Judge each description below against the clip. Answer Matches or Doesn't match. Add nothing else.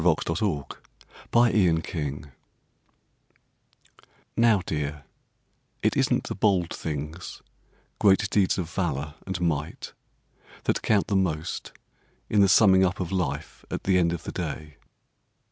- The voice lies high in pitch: Doesn't match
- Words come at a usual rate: Doesn't match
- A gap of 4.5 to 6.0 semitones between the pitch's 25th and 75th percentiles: Doesn't match